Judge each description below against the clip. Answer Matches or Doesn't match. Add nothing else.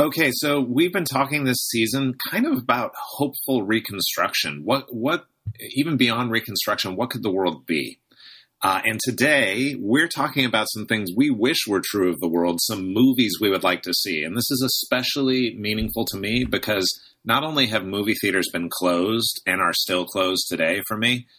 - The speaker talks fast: Doesn't match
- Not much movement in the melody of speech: Doesn't match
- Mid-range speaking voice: Doesn't match